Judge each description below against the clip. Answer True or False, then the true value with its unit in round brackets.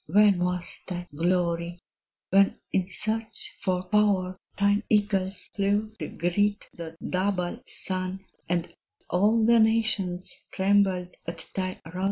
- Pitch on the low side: False (190 Hz)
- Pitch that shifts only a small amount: True (2.3 semitones)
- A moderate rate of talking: False (125 wpm)